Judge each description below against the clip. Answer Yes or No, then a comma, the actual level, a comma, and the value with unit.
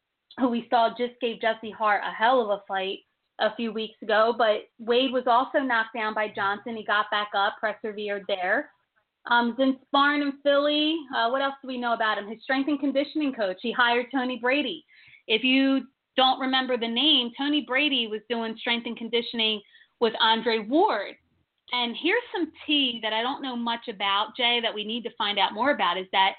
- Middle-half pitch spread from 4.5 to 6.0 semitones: No, average, 3.3 semitones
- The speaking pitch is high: Yes, high, 235 Hz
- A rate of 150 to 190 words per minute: No, average, 200 wpm